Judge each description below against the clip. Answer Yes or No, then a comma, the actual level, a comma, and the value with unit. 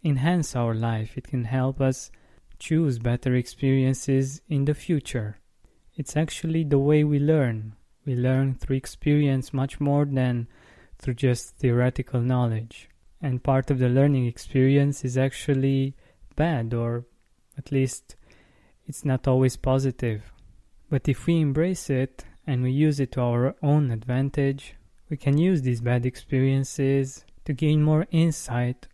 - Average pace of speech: Yes, average, 145 wpm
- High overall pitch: No, low, 135 Hz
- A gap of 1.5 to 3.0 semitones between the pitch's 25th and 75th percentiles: Yes, average, 2.7 semitones